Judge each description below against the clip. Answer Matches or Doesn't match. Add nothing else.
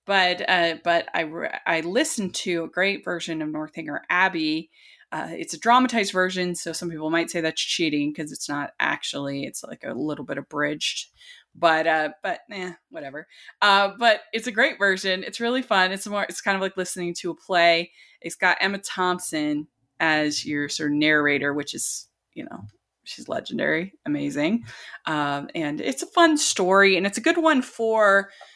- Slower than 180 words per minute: Doesn't match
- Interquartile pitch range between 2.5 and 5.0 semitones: Matches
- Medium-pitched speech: Matches